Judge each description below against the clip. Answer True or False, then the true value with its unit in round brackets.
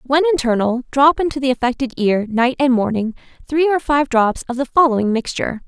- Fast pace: False (190 wpm)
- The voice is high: True (260 Hz)